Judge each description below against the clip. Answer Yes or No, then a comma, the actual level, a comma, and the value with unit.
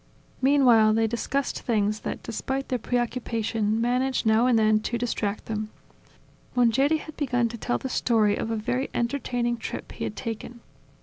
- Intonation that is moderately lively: No, narrow, 2.3 semitones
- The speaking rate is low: No, average, 165 wpm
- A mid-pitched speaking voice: No, high, 235 Hz